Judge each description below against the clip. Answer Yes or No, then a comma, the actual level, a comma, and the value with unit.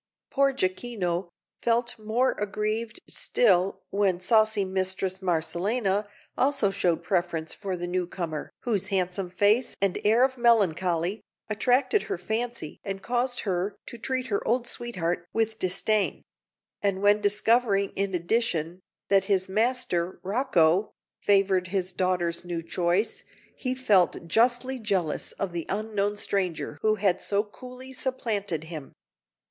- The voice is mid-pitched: No, high, 200 Hz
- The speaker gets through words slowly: Yes, slow, 130 wpm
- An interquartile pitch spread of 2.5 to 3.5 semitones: No, average, 4.0 semitones